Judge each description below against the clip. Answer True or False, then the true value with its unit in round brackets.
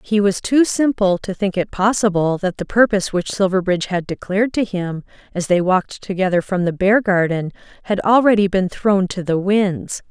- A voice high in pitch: True (195 Hz)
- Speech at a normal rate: True (185 wpm)